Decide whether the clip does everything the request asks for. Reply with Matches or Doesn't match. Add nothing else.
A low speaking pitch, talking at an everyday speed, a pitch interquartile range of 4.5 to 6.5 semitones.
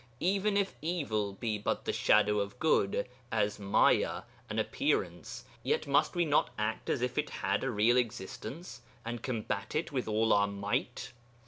Matches